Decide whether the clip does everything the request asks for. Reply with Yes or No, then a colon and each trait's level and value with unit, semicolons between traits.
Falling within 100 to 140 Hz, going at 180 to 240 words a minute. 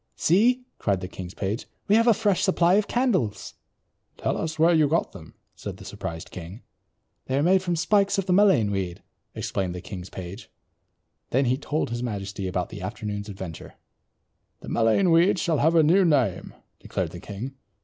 Yes: low, 135 Hz; average, 185 wpm